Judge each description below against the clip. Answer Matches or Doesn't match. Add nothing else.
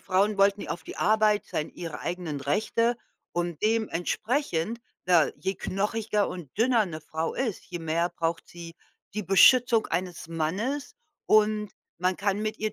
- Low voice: Doesn't match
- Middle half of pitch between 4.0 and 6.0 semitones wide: Matches